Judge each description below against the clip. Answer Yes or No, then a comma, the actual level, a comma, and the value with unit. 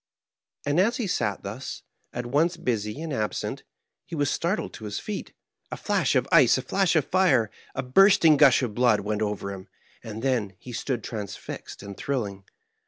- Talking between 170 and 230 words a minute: Yes, average, 180 wpm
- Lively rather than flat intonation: Yes, wide, 7.0 semitones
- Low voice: Yes, low, 125 Hz